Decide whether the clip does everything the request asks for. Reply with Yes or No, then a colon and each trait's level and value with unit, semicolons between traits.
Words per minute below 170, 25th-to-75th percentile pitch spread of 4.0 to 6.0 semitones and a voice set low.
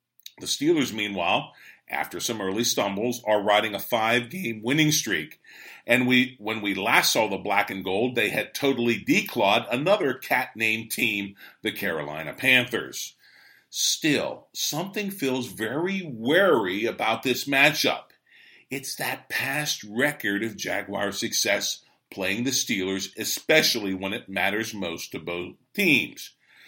Yes: slow, 135 wpm; average, 4.5 semitones; low, 115 Hz